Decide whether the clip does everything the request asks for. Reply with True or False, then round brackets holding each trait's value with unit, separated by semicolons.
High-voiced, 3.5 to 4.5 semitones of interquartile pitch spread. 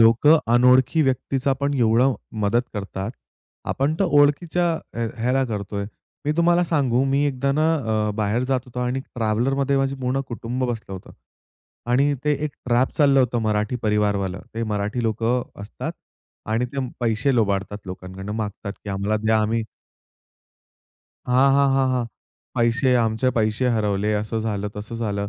False (120 Hz; 4.0 semitones)